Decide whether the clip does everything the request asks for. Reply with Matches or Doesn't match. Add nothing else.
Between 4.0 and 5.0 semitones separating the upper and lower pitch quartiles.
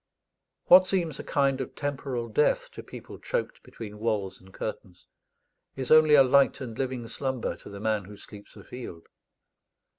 Matches